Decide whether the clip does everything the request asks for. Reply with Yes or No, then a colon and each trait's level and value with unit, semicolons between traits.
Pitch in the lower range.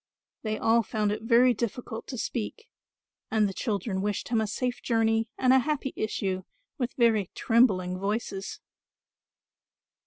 No: high, 225 Hz